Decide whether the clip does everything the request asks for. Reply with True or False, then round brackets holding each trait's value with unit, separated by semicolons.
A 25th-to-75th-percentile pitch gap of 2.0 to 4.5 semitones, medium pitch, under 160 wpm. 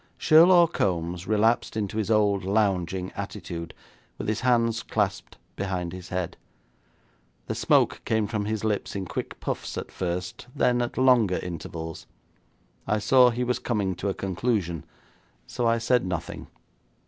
False (4.1 semitones; 105 Hz; 150 wpm)